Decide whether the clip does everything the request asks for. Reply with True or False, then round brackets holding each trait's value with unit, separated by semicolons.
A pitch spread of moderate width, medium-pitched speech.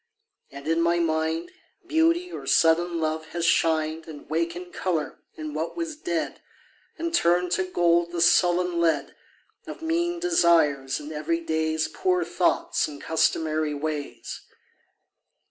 False (2.2 semitones; 165 Hz)